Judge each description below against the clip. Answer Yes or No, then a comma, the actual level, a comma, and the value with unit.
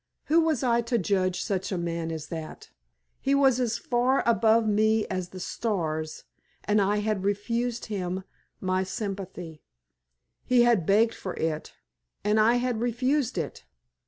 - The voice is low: No, high, 210 Hz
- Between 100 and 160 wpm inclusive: Yes, average, 155 wpm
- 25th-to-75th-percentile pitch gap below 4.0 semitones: No, average, 4.3 semitones